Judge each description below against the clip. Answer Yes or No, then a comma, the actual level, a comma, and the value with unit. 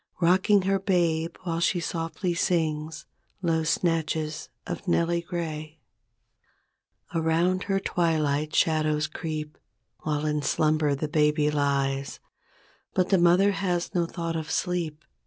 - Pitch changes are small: Yes, narrow, 2.3 semitones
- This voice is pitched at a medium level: Yes, medium, 160 Hz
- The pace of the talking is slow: Yes, slow, 120 wpm